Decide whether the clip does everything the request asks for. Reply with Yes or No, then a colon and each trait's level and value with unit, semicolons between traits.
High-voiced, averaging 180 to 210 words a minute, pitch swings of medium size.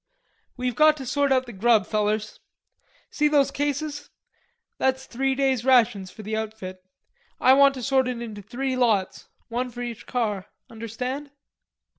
No: very high, 250 Hz; average, 155 wpm; average, 3.6 semitones